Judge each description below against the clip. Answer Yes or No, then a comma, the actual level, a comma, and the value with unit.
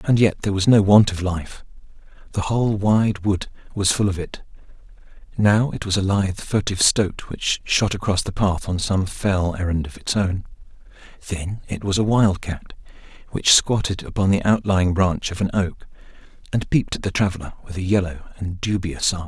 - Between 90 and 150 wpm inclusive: No, average, 185 wpm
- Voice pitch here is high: No, very low, 95 Hz